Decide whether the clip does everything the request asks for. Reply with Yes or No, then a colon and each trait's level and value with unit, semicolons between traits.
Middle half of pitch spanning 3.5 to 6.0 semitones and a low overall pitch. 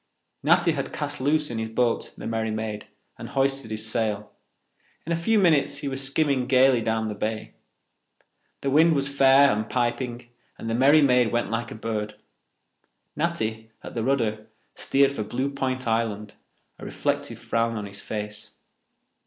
Yes: average, 3.8 semitones; low, 120 Hz